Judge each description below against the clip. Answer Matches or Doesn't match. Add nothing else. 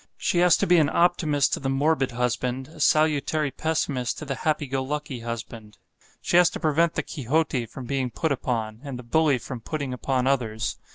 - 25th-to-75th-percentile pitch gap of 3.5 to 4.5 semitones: Matches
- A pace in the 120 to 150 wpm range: Doesn't match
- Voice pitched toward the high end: Doesn't match